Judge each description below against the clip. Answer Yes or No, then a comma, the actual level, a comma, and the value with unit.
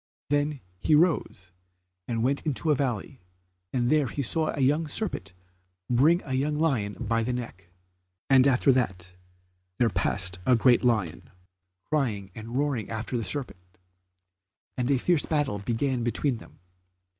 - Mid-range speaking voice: No, low, 125 Hz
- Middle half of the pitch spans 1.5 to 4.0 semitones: No, average, 4.6 semitones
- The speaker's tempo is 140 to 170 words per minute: Yes, average, 150 wpm